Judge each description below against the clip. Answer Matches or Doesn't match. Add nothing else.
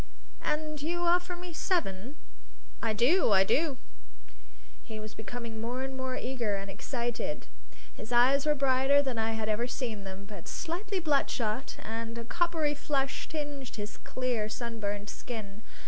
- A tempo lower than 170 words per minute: Matches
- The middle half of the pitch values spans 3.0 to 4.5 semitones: Doesn't match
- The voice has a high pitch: Matches